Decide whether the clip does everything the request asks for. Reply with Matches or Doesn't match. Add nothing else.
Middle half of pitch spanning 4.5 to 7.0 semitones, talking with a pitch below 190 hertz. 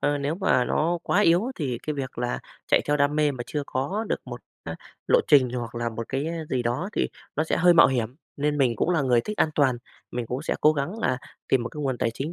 Doesn't match